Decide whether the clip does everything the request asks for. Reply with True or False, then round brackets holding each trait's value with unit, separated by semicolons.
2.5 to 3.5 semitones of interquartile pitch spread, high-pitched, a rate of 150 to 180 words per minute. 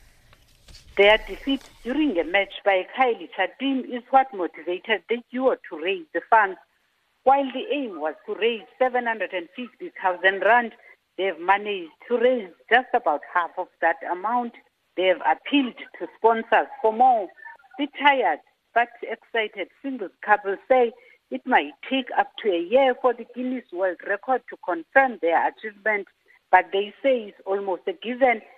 False (5.5 semitones; 230 Hz; 155 wpm)